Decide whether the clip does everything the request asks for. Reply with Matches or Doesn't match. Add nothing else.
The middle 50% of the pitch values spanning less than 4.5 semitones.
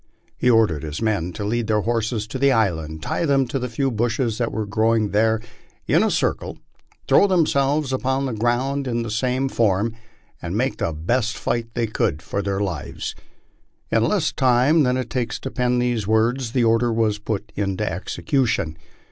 Matches